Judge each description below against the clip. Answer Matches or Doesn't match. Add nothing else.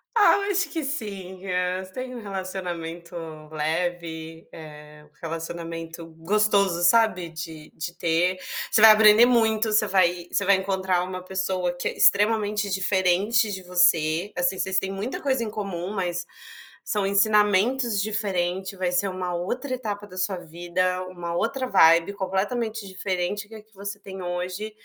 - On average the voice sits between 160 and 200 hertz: Matches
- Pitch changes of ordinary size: Matches